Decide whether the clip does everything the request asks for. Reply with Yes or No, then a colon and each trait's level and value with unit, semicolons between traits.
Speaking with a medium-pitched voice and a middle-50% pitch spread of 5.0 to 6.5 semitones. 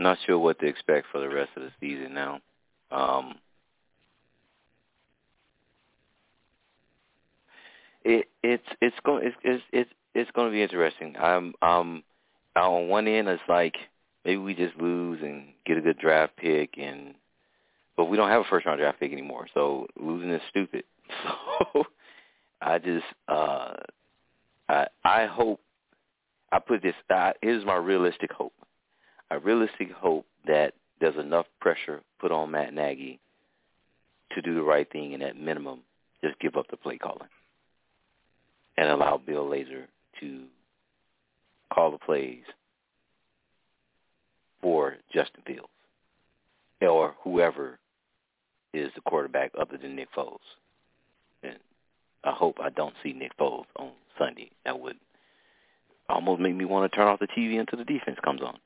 No: very low, 80 Hz; wide, 5.5 semitones